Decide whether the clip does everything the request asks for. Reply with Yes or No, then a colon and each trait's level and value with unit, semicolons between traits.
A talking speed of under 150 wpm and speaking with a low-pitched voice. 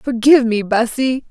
No: average, 140 wpm; high, 240 Hz